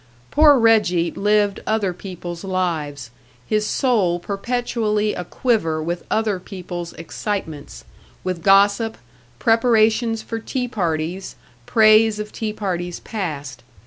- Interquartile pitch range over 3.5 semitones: Yes, average, 4.2 semitones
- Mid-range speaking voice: No, high, 200 Hz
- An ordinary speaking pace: No, slow, 110 wpm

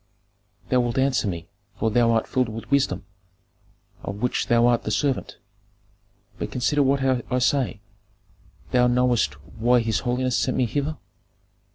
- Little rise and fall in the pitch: Yes, narrow, 2.3 semitones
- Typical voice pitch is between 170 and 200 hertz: No, low, 125 Hz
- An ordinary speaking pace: Yes, average, 150 wpm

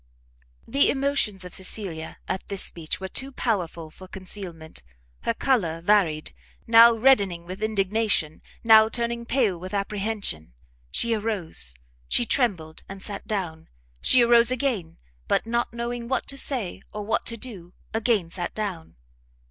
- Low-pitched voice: No, high, 210 Hz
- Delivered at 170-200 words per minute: No, average, 145 wpm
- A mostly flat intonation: No, average, 5.0 semitones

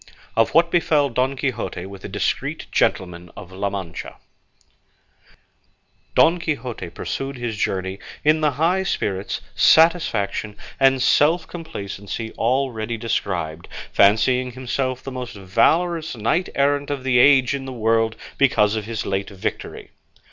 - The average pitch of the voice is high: No, low, 125 Hz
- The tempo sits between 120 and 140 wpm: Yes, slow, 135 wpm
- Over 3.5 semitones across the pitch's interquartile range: Yes, wide, 5.6 semitones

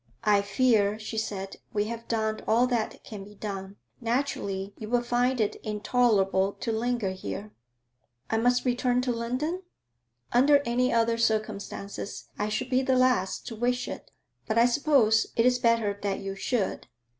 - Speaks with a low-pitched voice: No, high, 230 Hz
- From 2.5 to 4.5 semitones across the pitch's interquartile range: Yes, average, 3.1 semitones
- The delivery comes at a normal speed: Yes, average, 165 wpm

